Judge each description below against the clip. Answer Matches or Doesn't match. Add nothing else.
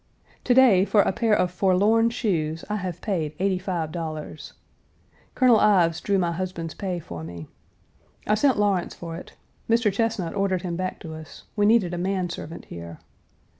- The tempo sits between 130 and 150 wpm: Doesn't match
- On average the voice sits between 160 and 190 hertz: Matches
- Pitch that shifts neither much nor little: Matches